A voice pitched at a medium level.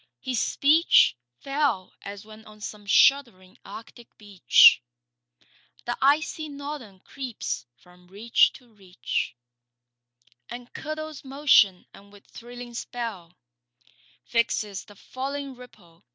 No: high, 235 Hz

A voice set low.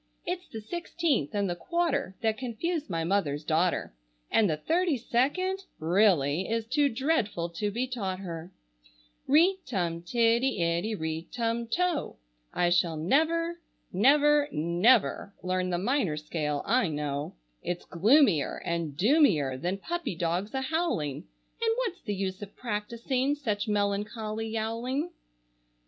No: high, 215 Hz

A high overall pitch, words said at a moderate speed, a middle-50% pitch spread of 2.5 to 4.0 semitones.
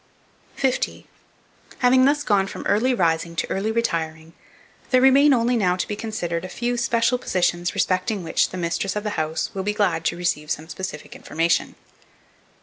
No: high, 195 Hz; average, 170 wpm; wide, 5.6 semitones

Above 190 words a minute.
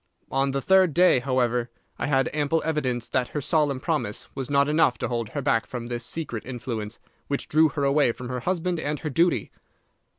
Yes: average, 200 wpm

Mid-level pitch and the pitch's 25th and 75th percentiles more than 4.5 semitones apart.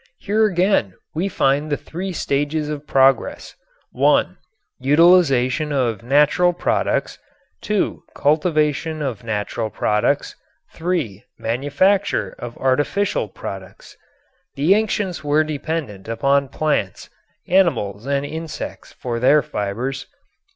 Yes: medium, 145 Hz; average, 5.1 semitones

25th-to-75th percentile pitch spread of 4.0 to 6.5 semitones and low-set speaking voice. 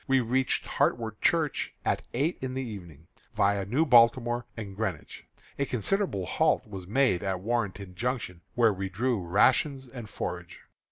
Yes: average, 4.9 semitones; low, 115 Hz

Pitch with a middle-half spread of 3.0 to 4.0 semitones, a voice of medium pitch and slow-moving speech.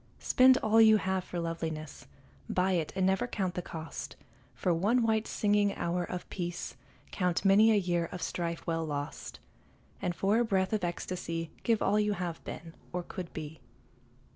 No: average, 3.6 semitones; medium, 180 Hz; average, 175 wpm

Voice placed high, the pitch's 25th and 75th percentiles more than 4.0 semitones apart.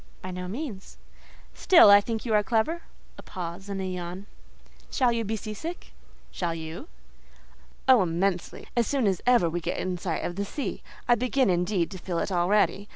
Yes: high, 200 Hz; average, 4.5 semitones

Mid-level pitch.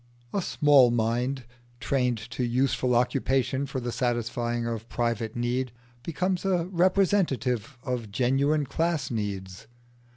No: low, 125 Hz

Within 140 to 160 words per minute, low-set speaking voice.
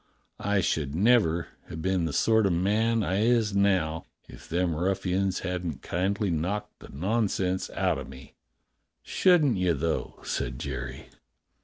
Yes: average, 145 wpm; very low, 95 Hz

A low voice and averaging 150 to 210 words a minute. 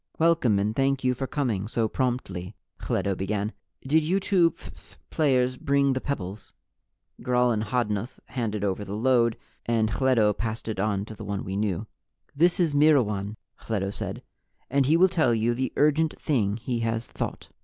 Yes: low, 120 Hz; average, 175 wpm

